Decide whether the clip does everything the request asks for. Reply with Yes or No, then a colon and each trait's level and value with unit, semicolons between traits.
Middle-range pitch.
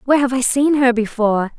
No: very high, 250 Hz